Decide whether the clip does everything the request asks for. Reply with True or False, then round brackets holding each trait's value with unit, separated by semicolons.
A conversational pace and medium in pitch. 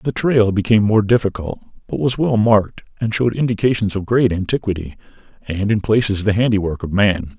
False (180 wpm; 105 Hz)